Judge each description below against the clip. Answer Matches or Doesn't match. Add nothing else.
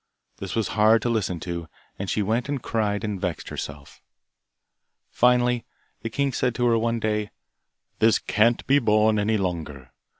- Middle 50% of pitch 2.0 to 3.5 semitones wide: Matches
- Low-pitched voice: Matches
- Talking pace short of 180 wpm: Matches